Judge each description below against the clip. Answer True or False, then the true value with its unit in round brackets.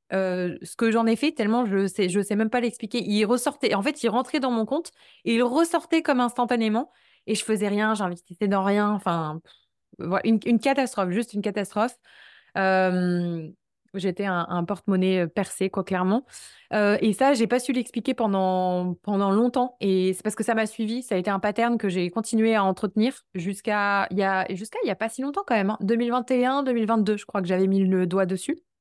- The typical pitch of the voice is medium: False (210 Hz)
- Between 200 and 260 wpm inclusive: True (210 wpm)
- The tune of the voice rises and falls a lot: False (3.7 semitones)